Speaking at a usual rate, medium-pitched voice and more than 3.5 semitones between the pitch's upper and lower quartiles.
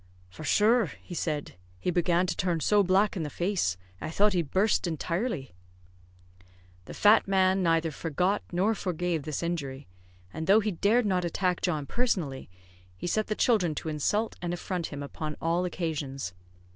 Yes: average, 170 wpm; medium, 175 Hz; average, 3.9 semitones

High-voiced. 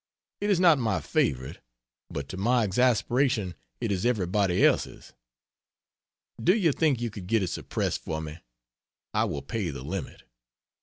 No: low, 105 Hz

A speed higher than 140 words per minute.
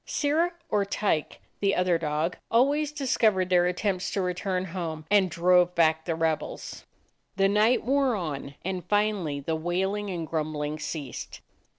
Yes: average, 155 wpm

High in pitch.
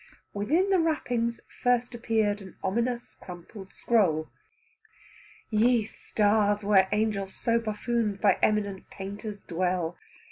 Yes: high, 210 Hz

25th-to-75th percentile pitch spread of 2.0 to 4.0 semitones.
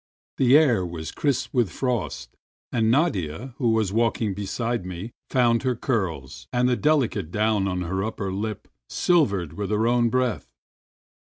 No: average, 4.6 semitones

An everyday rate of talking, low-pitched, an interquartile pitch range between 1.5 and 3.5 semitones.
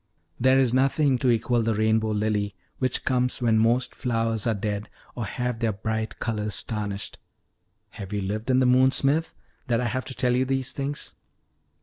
Yes: average, 185 wpm; low, 115 Hz; average, 2.9 semitones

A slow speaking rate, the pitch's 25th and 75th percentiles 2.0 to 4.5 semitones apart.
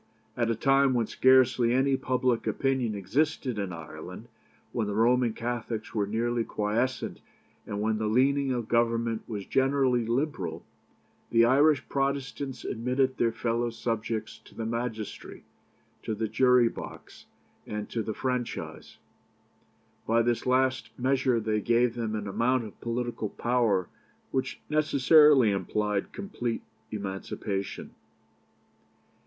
Yes: slow, 125 wpm; average, 3.0 semitones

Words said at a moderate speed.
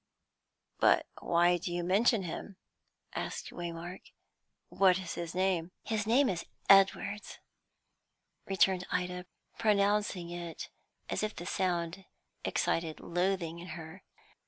No: slow, 115 wpm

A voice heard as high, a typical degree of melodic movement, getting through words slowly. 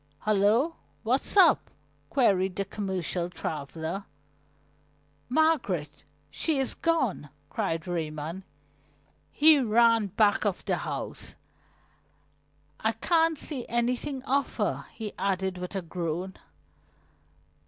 No: high, 205 Hz; wide, 6.5 semitones; slow, 100 wpm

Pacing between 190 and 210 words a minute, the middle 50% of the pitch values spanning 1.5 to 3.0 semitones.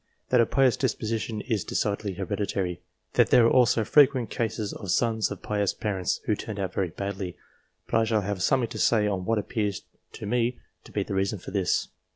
Yes: average, 200 wpm; average, 2.7 semitones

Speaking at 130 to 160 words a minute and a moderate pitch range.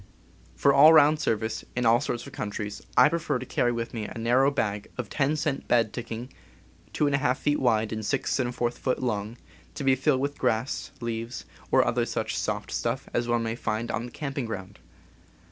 No: average, 195 wpm; average, 3.3 semitones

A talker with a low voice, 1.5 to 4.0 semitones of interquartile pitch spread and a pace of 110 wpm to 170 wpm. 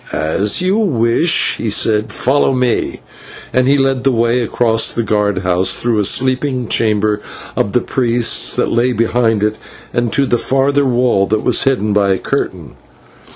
Yes: low, 120 Hz; average, 3.5 semitones; average, 165 wpm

